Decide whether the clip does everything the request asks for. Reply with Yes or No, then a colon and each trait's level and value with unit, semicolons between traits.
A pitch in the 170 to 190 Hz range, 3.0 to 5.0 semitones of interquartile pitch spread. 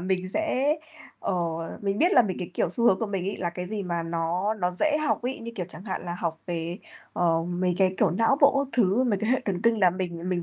Yes: medium, 185 Hz; average, 4.5 semitones